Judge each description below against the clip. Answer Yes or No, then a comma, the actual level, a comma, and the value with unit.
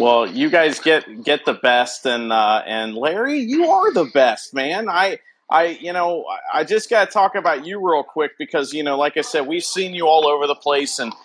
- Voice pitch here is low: No, medium, 155 Hz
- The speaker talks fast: Yes, fast, 225 wpm